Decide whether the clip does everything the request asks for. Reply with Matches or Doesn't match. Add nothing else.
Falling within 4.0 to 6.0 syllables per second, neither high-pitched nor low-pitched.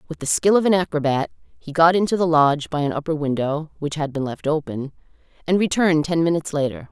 Doesn't match